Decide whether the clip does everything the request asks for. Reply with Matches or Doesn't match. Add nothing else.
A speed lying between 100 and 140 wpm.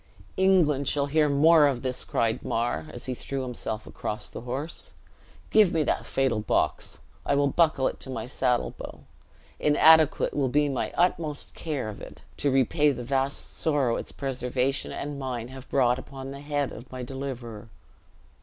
Doesn't match